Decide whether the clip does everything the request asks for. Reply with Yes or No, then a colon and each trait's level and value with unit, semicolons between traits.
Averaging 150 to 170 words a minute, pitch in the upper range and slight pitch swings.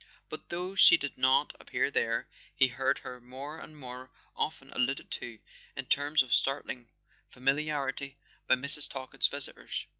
No: average, 155 wpm; low, 135 Hz; narrow, 2.0 semitones